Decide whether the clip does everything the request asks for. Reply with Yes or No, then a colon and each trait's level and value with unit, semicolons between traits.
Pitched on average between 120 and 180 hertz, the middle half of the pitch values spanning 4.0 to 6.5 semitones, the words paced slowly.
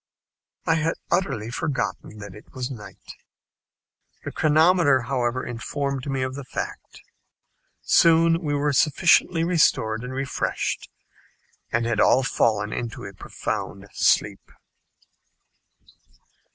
Yes: low, 135 Hz; average, 5.0 semitones; slow, 110 wpm